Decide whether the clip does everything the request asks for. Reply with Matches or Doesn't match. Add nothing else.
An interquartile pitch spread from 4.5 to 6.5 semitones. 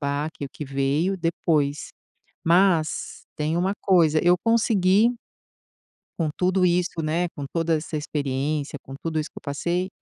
Doesn't match